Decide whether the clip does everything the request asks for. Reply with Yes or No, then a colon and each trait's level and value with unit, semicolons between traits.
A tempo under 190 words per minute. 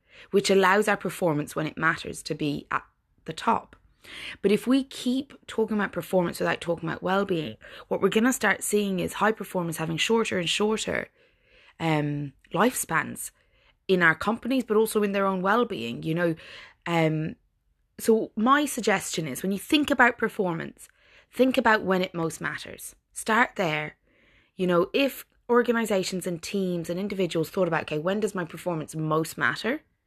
Yes: average, 170 wpm